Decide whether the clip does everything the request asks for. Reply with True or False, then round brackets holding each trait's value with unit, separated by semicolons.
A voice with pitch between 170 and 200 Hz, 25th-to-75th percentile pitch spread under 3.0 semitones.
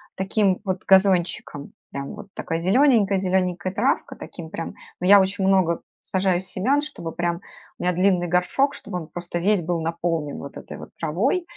True (185 Hz; 2.5 semitones)